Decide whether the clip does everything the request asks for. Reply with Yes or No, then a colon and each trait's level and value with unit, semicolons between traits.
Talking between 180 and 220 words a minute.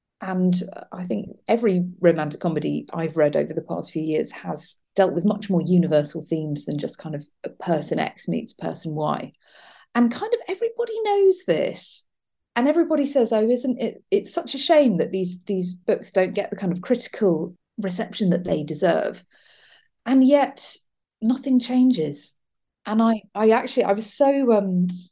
No: average, 170 wpm